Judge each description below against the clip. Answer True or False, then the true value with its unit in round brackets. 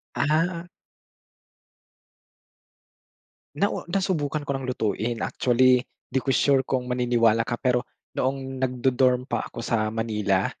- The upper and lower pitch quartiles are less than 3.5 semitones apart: True (2.8 semitones)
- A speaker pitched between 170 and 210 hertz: False (130 Hz)